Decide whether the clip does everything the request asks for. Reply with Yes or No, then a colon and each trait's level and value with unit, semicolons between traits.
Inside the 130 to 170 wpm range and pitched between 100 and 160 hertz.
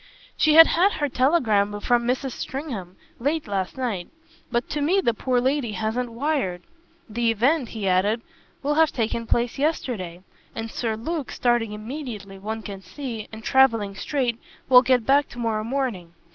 No: average, 160 wpm; high, 235 Hz